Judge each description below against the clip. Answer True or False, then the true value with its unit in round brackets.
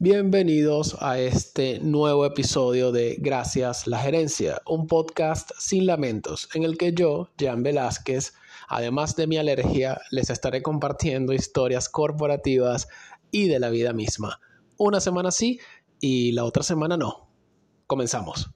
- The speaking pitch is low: False (145 Hz)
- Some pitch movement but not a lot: True (4.3 semitones)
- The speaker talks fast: False (135 wpm)